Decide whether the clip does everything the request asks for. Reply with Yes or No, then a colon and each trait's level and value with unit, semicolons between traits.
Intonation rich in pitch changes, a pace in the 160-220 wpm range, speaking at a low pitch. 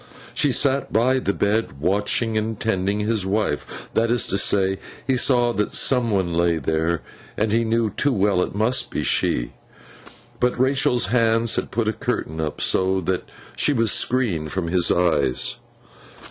No: average, 4.2 semitones; average, 170 wpm; low, 105 Hz